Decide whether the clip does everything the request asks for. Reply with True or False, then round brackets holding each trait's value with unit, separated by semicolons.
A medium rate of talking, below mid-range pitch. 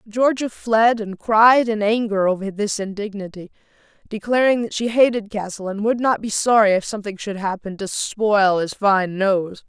False (175 wpm; 210 Hz)